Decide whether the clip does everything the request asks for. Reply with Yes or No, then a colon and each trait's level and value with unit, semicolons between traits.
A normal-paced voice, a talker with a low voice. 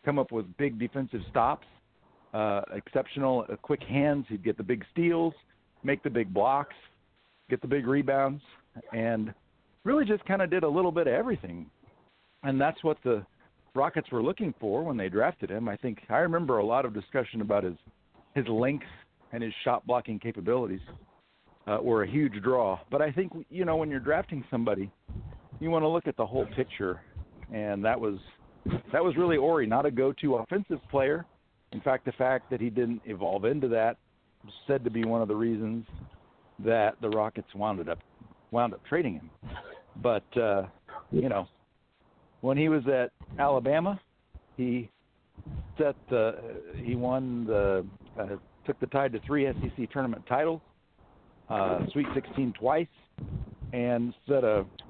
Yes: average, 170 wpm; low, 125 Hz